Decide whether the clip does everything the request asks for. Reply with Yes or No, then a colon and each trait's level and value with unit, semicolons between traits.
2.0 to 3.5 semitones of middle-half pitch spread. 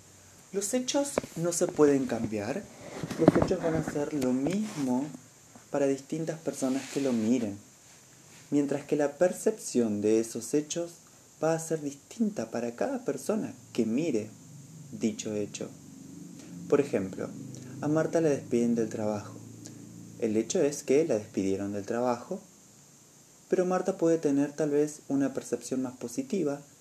No: average, 5.1 semitones